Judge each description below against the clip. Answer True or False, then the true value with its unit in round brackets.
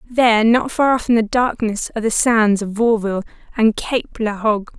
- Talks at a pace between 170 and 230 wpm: True (200 wpm)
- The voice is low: False (225 Hz)